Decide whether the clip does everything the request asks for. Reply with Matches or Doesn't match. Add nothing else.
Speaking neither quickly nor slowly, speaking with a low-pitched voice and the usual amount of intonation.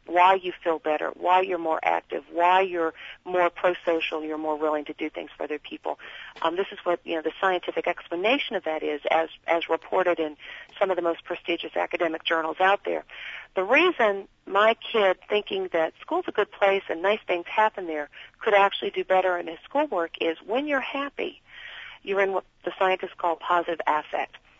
Doesn't match